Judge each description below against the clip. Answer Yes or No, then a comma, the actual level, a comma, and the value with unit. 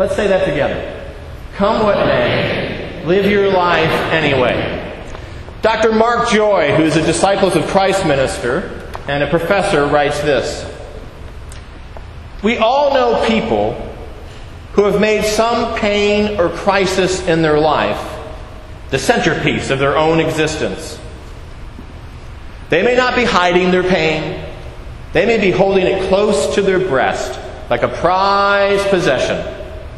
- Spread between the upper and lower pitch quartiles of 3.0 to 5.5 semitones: Yes, average, 4.7 semitones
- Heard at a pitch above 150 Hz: Yes, high, 190 Hz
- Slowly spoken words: Yes, slow, 130 wpm